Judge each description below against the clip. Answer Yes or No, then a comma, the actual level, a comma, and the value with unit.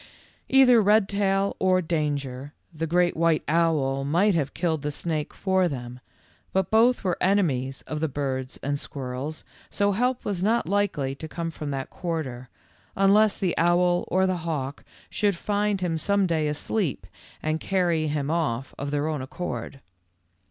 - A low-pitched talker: No, medium, 165 Hz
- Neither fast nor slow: Yes, average, 160 wpm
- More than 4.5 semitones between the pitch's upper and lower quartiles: Yes, average, 5.1 semitones